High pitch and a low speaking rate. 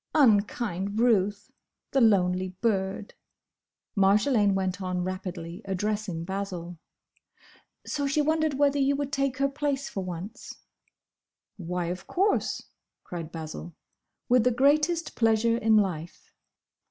Yes: high, 205 Hz; slow, 115 wpm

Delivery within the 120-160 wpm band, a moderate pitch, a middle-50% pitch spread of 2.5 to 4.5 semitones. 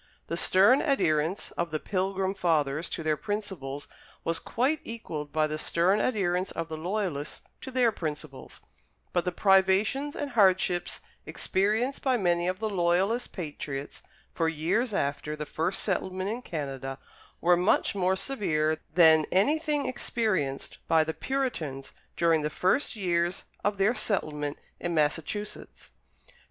No: average, 140 wpm; medium, 180 Hz; average, 5.1 semitones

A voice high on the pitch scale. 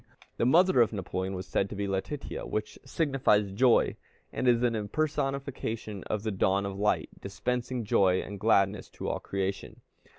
No: low, 105 Hz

